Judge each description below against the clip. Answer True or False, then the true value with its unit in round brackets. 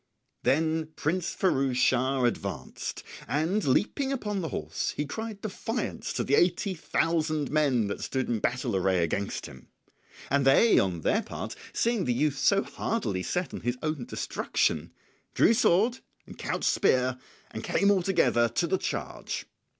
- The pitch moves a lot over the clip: True (7.2 semitones)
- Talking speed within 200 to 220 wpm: False (160 wpm)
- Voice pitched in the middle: True (155 Hz)